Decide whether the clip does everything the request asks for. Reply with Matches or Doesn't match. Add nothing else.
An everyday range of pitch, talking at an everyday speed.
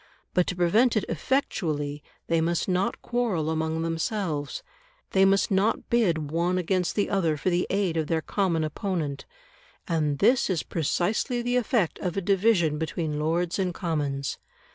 Matches